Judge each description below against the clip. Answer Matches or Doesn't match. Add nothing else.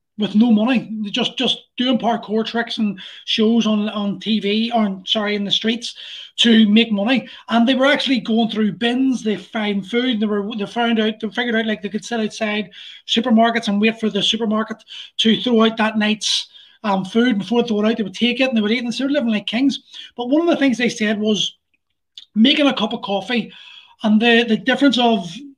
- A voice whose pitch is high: Matches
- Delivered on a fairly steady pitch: Matches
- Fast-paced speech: Matches